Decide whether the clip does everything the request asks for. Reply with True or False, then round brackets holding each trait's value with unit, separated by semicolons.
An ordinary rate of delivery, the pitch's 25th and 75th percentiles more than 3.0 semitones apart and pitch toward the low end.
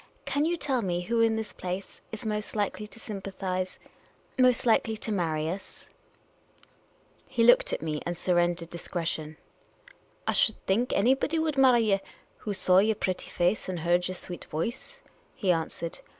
False (180 wpm; 4.5 semitones; 195 Hz)